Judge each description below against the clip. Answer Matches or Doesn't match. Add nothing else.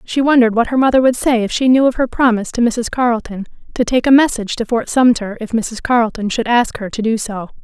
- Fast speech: Matches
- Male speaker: Doesn't match